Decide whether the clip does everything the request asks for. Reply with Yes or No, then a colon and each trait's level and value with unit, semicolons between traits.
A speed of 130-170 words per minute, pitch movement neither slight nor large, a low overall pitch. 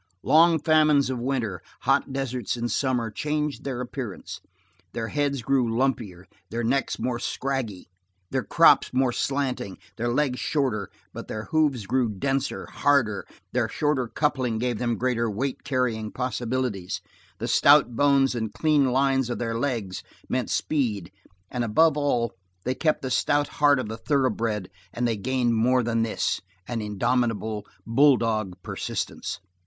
Yes: average, 150 wpm; average, 3.4 semitones; low, 125 Hz